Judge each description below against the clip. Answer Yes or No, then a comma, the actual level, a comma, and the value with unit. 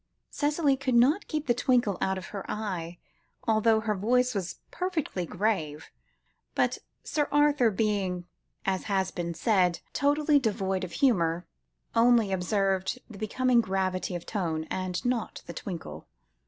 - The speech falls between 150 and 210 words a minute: No, average, 140 wpm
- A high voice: Yes, high, 210 Hz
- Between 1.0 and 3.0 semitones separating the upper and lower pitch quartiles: No, average, 5.3 semitones